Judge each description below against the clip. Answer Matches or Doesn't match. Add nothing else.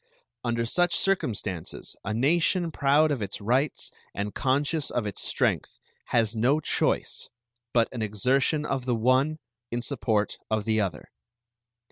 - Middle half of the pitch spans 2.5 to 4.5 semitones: Doesn't match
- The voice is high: Doesn't match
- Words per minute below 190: Matches